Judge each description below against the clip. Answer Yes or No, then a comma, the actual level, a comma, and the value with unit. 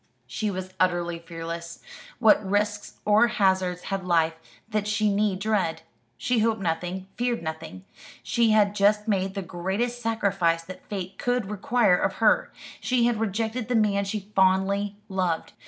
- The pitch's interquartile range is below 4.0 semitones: Yes, average, 2.9 semitones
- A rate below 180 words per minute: Yes, average, 155 wpm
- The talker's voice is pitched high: Yes, high, 200 Hz